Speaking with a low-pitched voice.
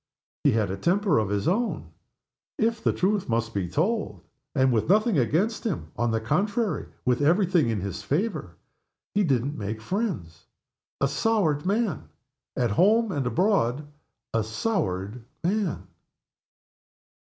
No: medium, 145 Hz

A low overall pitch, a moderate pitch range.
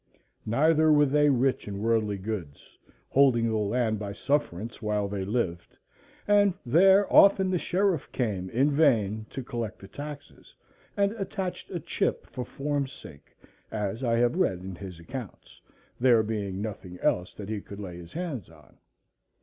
No: low, 115 Hz; wide, 6.5 semitones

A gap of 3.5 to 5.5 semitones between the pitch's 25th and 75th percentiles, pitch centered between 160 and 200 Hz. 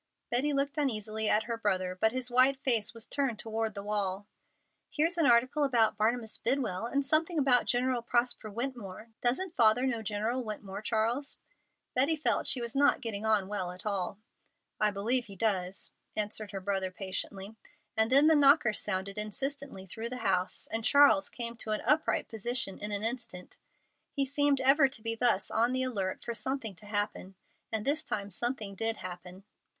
No: average, 4.1 semitones; high, 225 Hz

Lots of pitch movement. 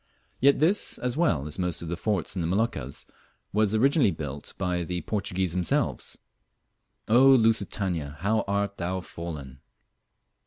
No: average, 4.7 semitones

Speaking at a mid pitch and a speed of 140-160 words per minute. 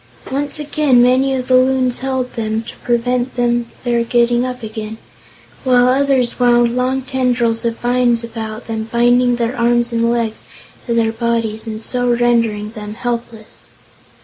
No: high, 240 Hz; average, 150 wpm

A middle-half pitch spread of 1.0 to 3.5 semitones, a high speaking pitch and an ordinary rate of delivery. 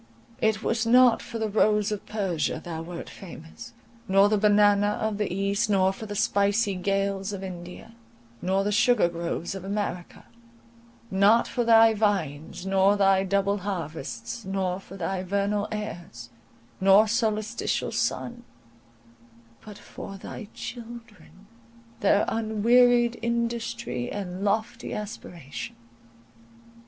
No: average, 2.9 semitones; high, 200 Hz; slow, 125 wpm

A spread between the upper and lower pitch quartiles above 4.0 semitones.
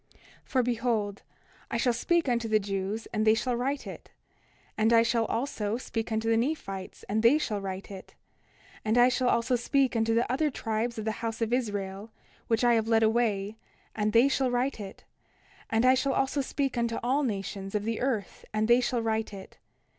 No: narrow, 2.4 semitones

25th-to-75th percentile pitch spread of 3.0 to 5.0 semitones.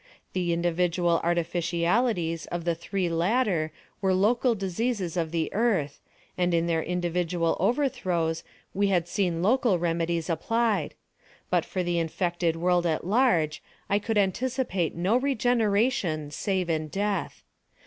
Yes: average, 3.5 semitones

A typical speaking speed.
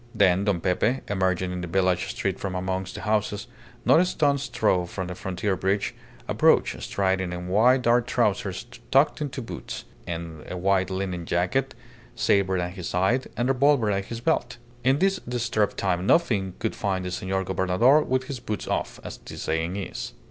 Yes: average, 175 wpm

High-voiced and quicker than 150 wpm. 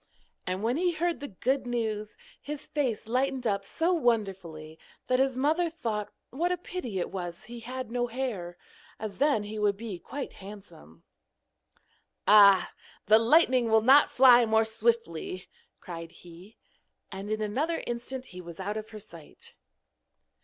Yes: high, 225 Hz; average, 160 wpm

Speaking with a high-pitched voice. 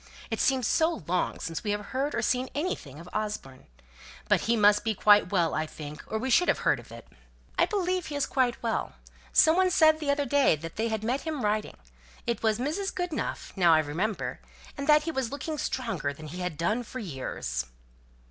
Yes: high, 225 Hz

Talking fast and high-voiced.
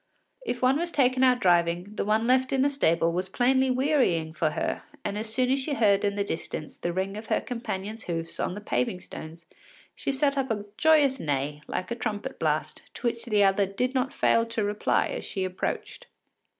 Yes: fast, 210 wpm; high, 215 Hz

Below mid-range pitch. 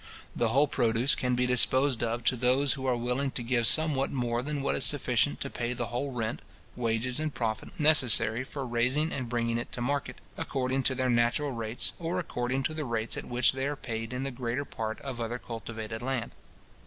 Yes: low, 125 Hz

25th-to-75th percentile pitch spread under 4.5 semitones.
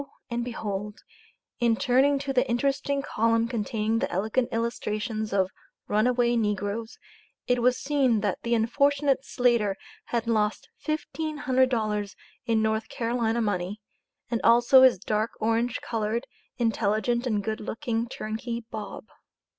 Yes: narrow, 2.4 semitones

